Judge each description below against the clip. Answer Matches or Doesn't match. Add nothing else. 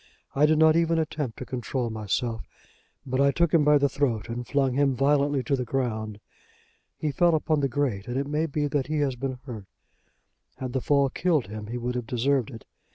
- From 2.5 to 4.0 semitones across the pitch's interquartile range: Matches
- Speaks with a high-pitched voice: Doesn't match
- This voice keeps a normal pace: Doesn't match